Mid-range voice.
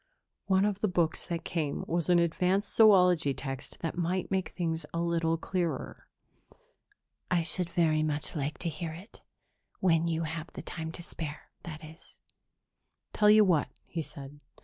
Yes: medium, 170 Hz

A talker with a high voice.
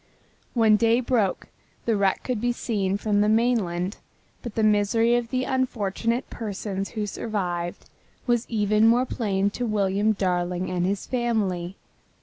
Yes: high, 210 Hz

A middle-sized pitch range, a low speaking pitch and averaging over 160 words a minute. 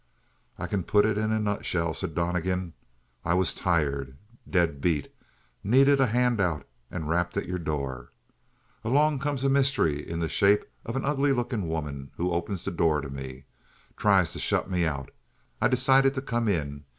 No: wide, 7.2 semitones; very low, 90 Hz; average, 175 wpm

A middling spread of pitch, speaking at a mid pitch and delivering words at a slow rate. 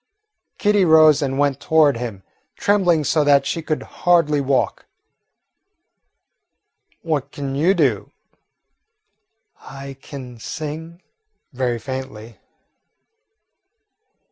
Yes: average, 3.3 semitones; medium, 145 Hz; slow, 90 wpm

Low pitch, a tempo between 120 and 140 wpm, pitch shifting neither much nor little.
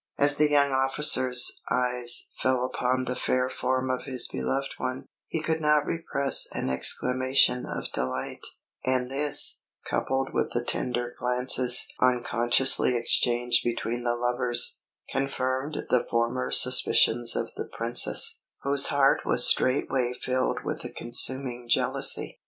No: low, 125 Hz; slow, 135 wpm; narrow, 1.7 semitones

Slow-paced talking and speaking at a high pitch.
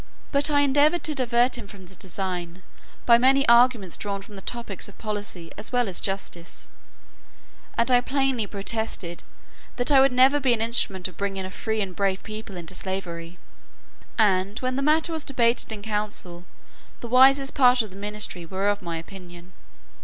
No: average, 180 wpm; high, 210 Hz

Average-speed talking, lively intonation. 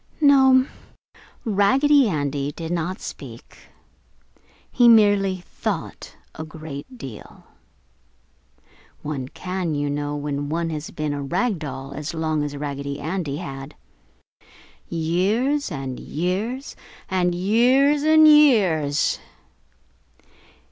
No: slow, 105 wpm; wide, 7.4 semitones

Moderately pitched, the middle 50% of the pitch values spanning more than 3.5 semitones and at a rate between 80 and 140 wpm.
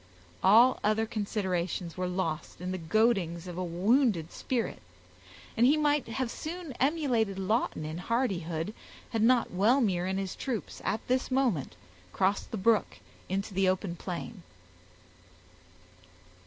No: high, 205 Hz; average, 4.9 semitones; slow, 135 wpm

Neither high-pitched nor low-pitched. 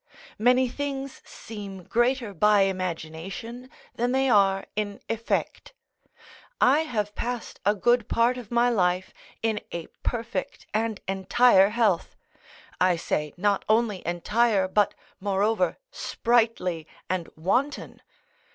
No: high, 210 Hz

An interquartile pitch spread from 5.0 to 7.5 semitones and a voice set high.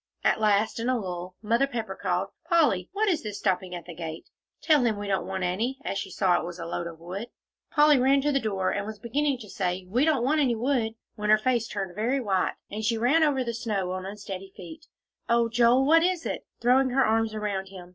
Yes: average, 5.3 semitones; high, 220 Hz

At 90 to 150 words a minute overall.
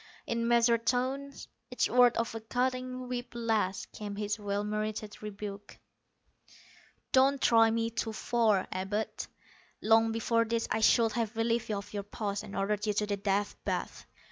No: average, 160 wpm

